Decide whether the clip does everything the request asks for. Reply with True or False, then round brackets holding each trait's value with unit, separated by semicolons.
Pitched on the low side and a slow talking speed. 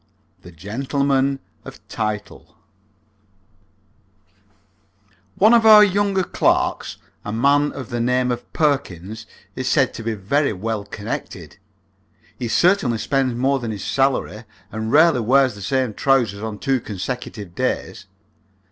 True (125 Hz; 130 wpm)